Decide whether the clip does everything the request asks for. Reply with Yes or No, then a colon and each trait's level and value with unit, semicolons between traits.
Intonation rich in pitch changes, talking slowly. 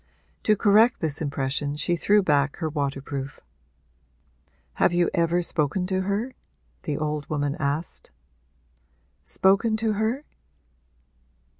Yes: wide, 5.7 semitones; slow, 115 wpm